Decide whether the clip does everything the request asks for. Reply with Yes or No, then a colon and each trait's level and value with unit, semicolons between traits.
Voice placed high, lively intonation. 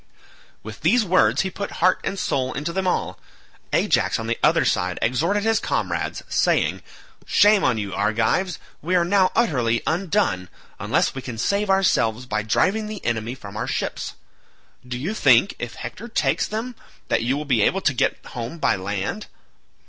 No: medium, 150 Hz; wide, 9.0 semitones